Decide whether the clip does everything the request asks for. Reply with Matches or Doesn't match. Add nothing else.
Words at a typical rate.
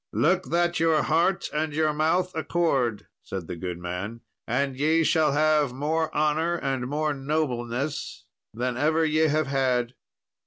Matches